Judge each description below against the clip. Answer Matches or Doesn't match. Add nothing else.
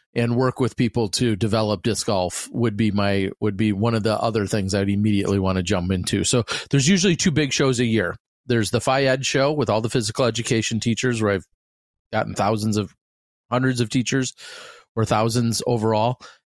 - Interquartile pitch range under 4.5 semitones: Matches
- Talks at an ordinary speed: Matches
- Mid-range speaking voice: Doesn't match